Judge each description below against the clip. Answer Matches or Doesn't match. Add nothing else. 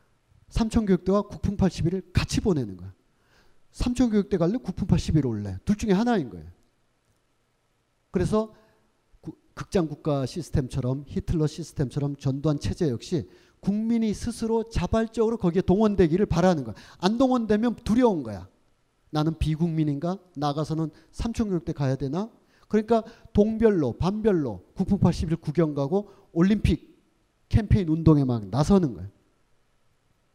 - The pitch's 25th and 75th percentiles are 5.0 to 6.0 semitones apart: Doesn't match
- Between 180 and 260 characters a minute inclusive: Doesn't match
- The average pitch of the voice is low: Doesn't match